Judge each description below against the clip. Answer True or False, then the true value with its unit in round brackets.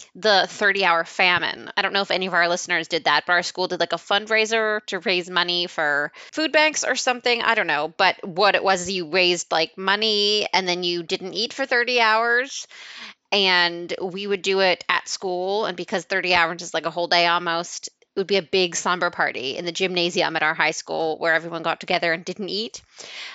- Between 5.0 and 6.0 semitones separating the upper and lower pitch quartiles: False (2.7 semitones)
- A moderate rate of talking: False (220 wpm)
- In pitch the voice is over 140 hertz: True (185 Hz)